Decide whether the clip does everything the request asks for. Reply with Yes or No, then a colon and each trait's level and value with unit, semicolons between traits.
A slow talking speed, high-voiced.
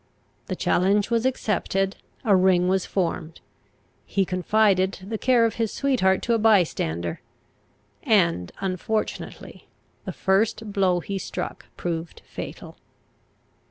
Yes: slow, 120 wpm; high, 195 Hz